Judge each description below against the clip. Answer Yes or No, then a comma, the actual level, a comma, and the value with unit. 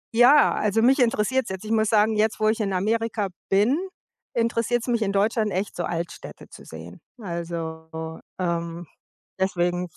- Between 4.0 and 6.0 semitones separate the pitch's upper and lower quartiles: Yes, average, 4.4 semitones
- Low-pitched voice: No, high, 210 Hz